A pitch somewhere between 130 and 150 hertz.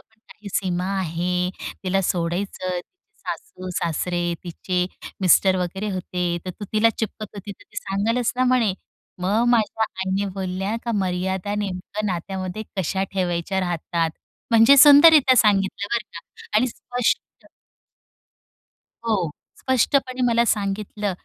No: high, 195 Hz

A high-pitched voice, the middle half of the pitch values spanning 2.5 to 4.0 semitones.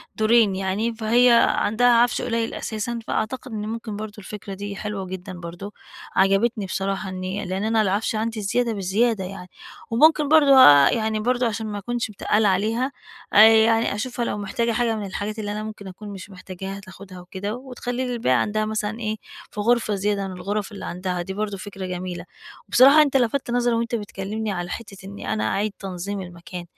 Yes: high, 210 Hz; average, 3.1 semitones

